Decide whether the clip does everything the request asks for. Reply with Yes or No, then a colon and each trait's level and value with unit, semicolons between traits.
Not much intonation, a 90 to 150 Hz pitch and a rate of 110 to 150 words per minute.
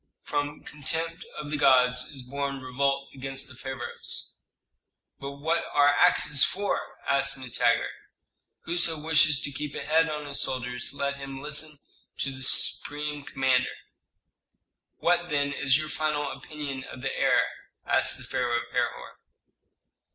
Yes: narrow, 2.2 semitones; medium, 140 Hz; average, 145 wpm